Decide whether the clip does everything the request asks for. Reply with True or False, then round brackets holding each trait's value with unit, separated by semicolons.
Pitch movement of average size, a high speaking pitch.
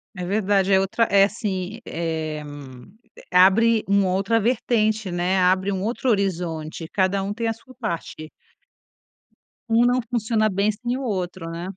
True (3.5 semitones; 200 Hz)